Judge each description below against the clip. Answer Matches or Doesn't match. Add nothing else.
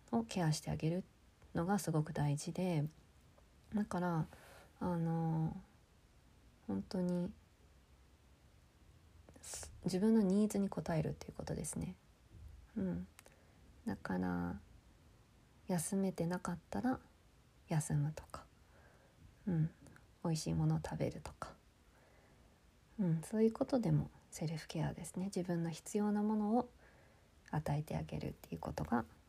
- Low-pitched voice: Doesn't match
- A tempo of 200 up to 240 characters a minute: Matches